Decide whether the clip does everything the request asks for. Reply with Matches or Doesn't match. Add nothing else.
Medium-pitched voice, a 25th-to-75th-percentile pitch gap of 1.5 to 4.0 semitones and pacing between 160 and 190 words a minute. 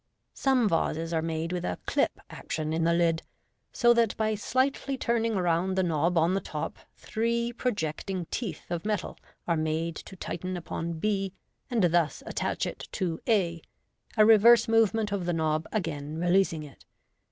Doesn't match